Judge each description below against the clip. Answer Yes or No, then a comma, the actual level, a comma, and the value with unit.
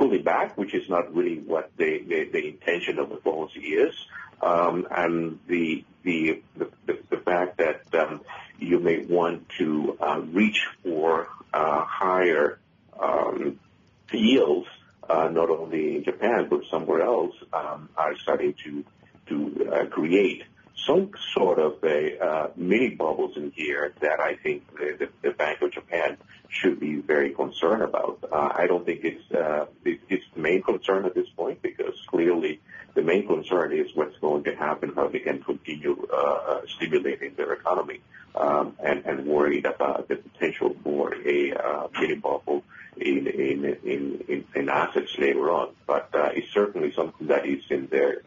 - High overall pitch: Yes, very high, 385 Hz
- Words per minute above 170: No, average, 165 wpm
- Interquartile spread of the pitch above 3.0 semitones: No, narrow, 2.6 semitones